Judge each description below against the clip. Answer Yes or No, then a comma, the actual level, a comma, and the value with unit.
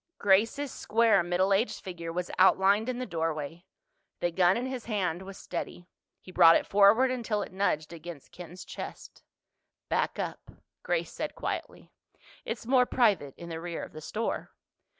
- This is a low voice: No, high, 190 Hz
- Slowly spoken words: No, average, 165 wpm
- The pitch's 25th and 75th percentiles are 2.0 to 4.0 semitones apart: No, average, 4.5 semitones